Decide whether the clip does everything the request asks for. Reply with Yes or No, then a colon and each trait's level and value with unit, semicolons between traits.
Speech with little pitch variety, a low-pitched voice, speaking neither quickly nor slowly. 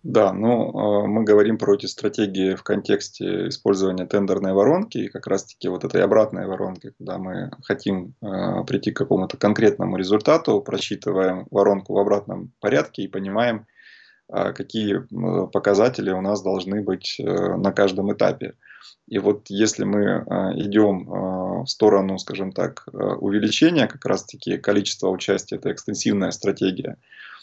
Yes: narrow, 1.7 semitones; low, 100 Hz; average, 135 wpm